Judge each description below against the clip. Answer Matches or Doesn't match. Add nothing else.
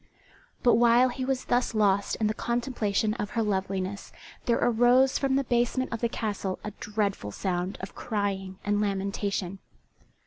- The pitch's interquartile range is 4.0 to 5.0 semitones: Doesn't match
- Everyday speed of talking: Matches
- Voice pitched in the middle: Doesn't match